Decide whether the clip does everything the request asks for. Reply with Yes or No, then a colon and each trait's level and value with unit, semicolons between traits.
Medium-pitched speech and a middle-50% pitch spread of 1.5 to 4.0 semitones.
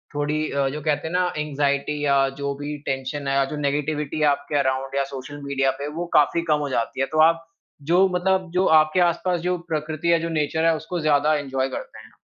Yes: medium, 150 Hz; narrow, 2.4 semitones